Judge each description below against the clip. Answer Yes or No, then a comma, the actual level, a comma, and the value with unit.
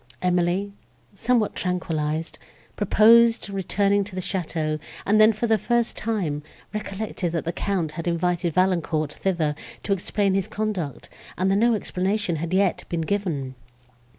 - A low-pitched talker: No, high, 190 Hz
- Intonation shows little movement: No, average, 3.4 semitones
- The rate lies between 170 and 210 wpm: No, average, 145 wpm